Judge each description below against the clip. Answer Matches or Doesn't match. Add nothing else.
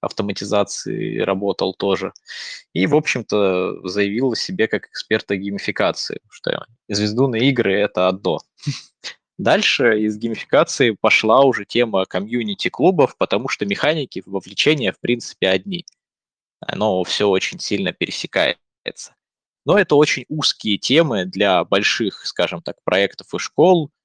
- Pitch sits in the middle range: Doesn't match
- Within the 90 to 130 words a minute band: Matches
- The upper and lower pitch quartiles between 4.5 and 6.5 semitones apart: Matches